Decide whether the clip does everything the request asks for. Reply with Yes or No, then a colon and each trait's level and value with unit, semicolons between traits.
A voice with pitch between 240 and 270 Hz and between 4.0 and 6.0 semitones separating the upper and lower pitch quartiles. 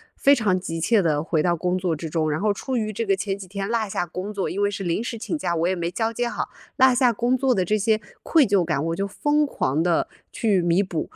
No: high, 195 Hz; average, 4.8 semitones